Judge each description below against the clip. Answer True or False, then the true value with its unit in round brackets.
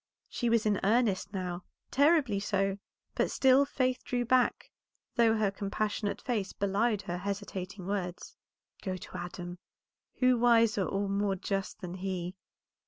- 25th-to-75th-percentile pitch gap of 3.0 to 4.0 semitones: True (3.5 semitones)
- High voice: True (200 Hz)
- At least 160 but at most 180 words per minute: False (140 wpm)